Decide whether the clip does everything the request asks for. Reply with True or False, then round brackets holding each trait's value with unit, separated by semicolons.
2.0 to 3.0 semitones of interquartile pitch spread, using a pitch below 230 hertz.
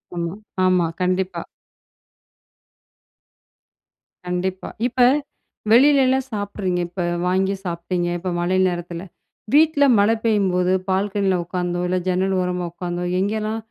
True (2.5 semitones; 185 Hz)